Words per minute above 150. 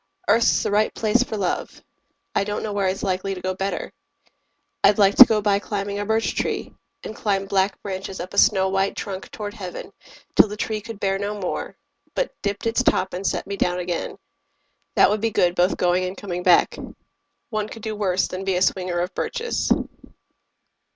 Yes: average, 200 wpm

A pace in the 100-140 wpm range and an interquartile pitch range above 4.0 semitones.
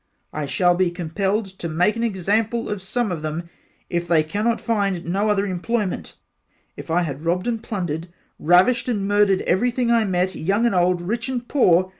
No: average, 185 wpm; average, 4.4 semitones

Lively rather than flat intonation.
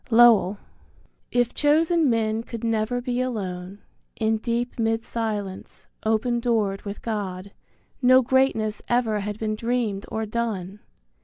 No: narrow, 2.5 semitones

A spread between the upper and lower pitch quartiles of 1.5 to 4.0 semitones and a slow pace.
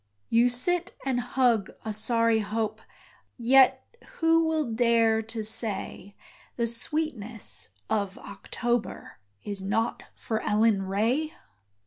Yes: narrow, 2.5 semitones; slow, 110 wpm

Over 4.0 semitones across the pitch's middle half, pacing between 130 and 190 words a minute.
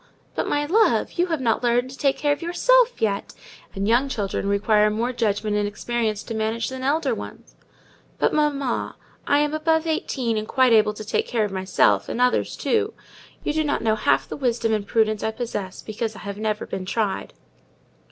No: average, 5.2 semitones; average, 200 wpm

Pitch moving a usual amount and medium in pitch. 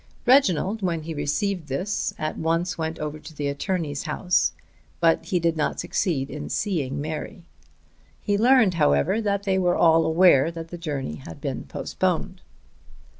Yes: average, 3.9 semitones; medium, 165 Hz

